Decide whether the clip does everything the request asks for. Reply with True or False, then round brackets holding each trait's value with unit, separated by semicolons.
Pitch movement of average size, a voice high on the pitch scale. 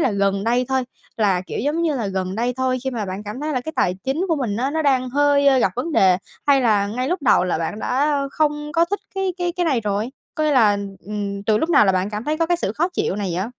False (6.5 semitones; 250 Hz)